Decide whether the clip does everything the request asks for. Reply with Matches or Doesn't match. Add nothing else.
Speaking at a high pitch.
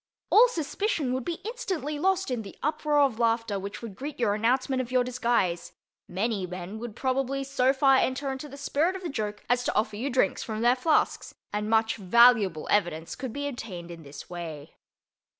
Matches